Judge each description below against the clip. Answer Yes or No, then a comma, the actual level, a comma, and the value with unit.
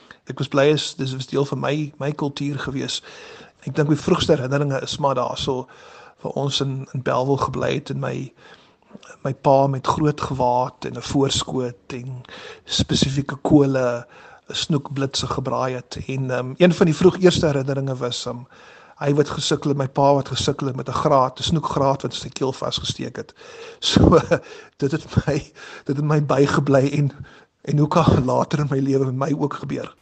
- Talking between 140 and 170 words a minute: No, average, 185 wpm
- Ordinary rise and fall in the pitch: No, narrow, 2.1 semitones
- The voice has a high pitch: No, medium, 140 Hz